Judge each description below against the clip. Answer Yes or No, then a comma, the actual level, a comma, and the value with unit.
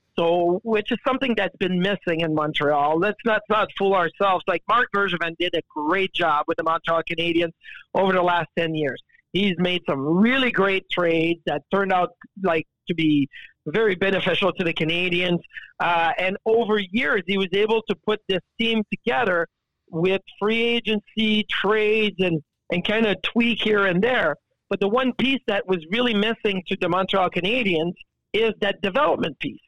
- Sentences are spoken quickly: No, average, 180 wpm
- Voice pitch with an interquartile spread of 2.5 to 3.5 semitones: No, average, 3.9 semitones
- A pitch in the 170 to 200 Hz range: Yes, high, 190 Hz